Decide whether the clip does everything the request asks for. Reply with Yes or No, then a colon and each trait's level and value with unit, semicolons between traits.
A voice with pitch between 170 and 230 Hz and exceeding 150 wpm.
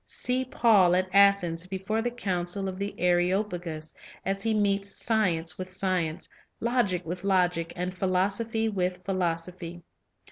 No: medium, 185 Hz; average, 140 wpm